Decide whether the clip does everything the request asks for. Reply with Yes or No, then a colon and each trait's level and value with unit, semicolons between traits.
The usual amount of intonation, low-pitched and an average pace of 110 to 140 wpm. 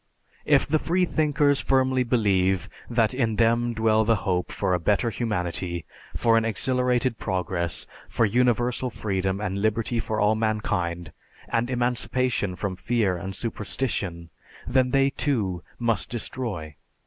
Yes: average, 4.6 semitones; low, 110 Hz; slow, 135 wpm